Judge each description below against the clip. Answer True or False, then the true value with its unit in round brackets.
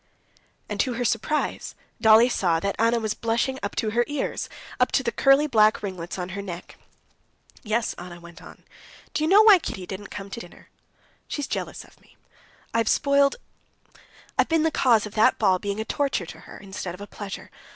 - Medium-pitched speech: False (220 Hz)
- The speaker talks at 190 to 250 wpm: True (200 wpm)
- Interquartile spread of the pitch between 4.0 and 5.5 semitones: True (5.2 semitones)